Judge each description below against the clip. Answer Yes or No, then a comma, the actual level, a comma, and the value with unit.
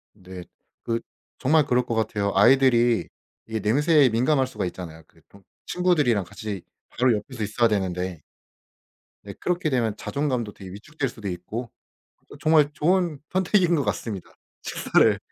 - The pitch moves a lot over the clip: Yes, wide, 6.4 semitones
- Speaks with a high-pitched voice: No, low, 120 Hz